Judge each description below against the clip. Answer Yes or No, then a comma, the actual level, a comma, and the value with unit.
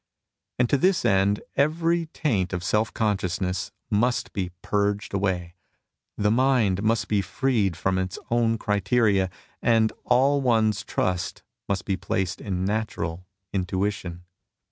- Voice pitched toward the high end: No, low, 105 Hz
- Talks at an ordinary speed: No, slow, 125 wpm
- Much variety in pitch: No, average, 3.9 semitones